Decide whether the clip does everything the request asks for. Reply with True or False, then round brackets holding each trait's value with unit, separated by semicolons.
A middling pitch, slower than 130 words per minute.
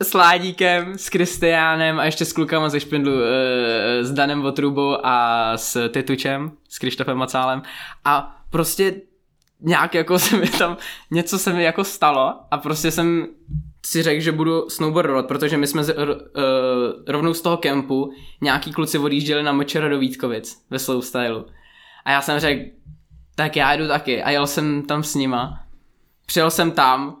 False (145 Hz; 170 wpm)